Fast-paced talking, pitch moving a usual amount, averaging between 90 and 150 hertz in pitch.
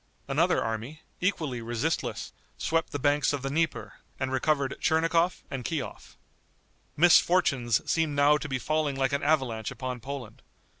No: average, 145 wpm; average, 3.4 semitones; medium, 140 Hz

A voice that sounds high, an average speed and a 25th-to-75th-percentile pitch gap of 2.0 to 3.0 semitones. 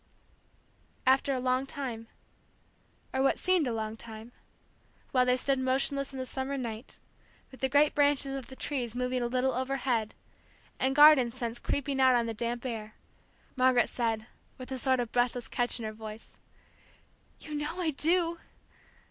Yes: very high, 255 Hz; average, 170 wpm; narrow, 2.4 semitones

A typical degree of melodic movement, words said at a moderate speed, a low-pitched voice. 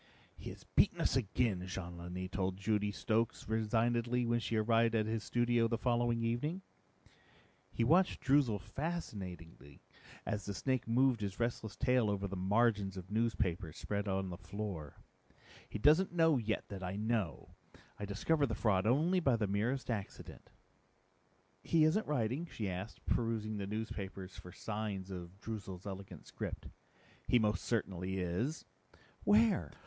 Yes: average, 3.7 semitones; average, 150 wpm; low, 110 Hz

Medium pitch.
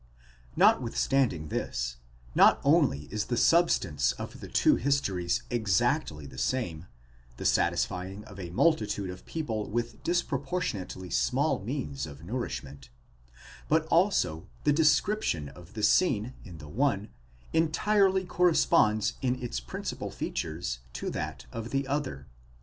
No: low, 105 Hz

